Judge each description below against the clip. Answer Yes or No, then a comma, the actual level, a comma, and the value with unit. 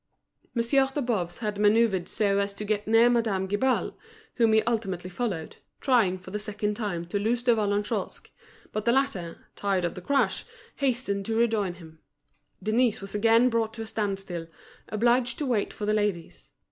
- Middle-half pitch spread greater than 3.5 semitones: No, average, 3.0 semitones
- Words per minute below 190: Yes, average, 175 wpm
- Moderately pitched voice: No, high, 215 Hz